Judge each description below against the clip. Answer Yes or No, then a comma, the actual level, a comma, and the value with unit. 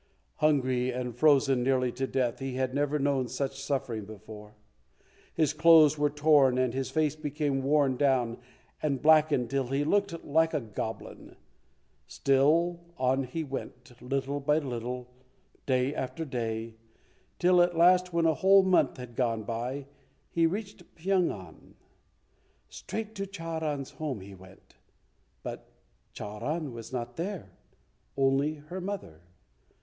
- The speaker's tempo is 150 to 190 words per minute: No, average, 140 wpm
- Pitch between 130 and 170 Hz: Yes, medium, 140 Hz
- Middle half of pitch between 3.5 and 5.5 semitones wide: Yes, average, 4.0 semitones